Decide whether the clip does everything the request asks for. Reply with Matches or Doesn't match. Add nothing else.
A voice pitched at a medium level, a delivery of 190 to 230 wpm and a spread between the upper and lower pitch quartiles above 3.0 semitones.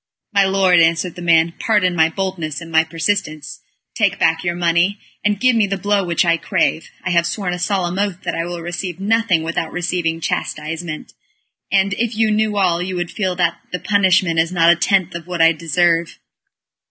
Doesn't match